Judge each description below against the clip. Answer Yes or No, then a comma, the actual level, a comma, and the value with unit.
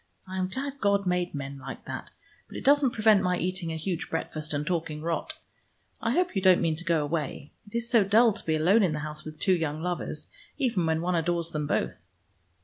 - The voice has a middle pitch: Yes, medium, 175 Hz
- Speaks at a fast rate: Yes, fast, 230 wpm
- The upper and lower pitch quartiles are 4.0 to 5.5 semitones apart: Yes, average, 4.5 semitones